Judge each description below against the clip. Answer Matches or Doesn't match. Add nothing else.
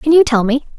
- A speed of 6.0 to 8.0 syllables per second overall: Matches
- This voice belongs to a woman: Matches